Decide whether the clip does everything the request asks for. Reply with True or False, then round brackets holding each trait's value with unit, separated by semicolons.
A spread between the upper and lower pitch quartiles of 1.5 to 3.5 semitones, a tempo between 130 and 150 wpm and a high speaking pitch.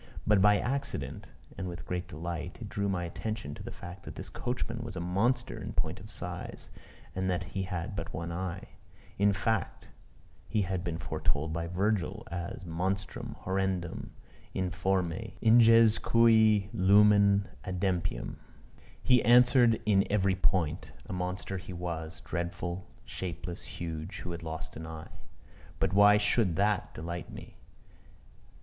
False (3.2 semitones; 145 wpm; 95 Hz)